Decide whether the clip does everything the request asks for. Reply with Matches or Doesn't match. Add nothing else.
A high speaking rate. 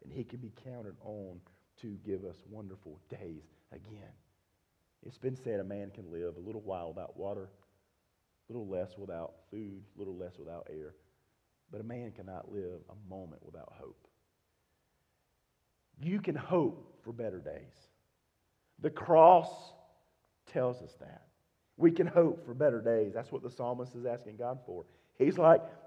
Doesn't match